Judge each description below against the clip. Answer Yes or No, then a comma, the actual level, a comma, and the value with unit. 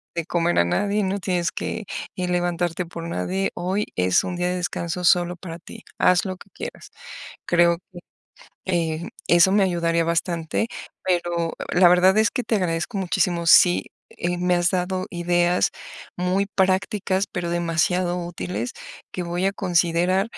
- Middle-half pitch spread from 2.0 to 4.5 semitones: No, narrow, 1.5 semitones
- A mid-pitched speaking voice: Yes, medium, 175 Hz